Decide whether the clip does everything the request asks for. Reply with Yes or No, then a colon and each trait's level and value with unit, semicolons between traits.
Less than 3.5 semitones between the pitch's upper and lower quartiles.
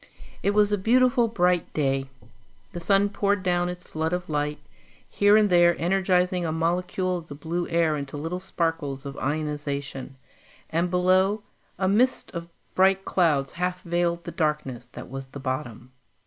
No: average, 3.8 semitones